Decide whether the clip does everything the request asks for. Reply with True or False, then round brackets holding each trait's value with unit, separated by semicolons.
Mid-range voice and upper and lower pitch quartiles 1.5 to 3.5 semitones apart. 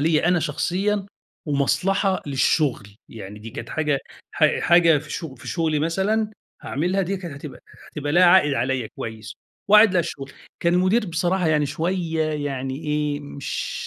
False (160 Hz; 4.3 semitones)